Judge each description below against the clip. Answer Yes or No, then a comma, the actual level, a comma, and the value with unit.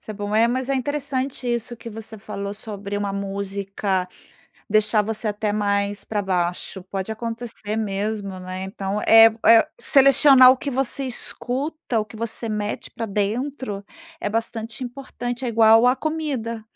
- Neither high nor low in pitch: No, high, 220 Hz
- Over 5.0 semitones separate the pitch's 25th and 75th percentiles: No, average, 3.3 semitones